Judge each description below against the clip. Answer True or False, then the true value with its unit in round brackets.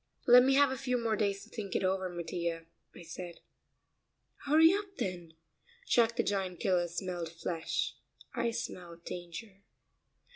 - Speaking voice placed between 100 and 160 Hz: False (190 Hz)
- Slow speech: False (150 wpm)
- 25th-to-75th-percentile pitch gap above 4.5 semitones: True (5.3 semitones)